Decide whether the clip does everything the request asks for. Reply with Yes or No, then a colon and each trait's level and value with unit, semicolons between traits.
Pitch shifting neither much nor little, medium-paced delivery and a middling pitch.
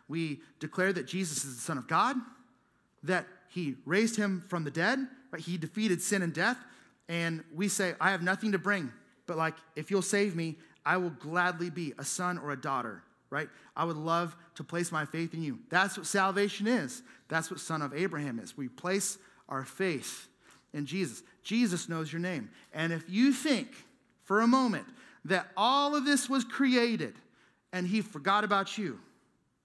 Yes: average, 4.2 semitones; average, 190 wpm; medium, 180 Hz